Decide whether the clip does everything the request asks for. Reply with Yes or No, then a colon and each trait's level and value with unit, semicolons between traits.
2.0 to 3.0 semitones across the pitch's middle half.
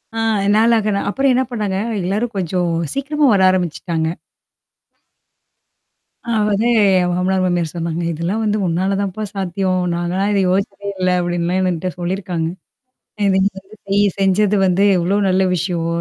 Yes: average, 2.7 semitones